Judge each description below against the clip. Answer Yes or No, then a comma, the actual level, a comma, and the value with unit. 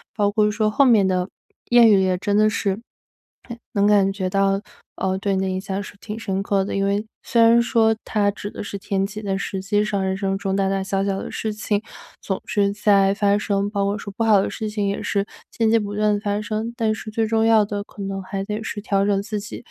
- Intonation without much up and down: Yes, narrow, 1.5 semitones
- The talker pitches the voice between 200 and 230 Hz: Yes, high, 205 Hz